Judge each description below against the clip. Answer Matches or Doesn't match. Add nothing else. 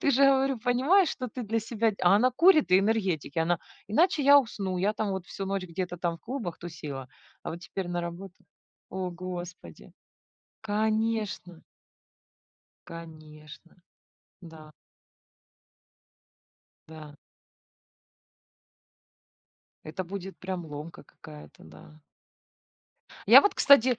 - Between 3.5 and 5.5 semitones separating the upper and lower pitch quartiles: Matches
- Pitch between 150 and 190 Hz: Matches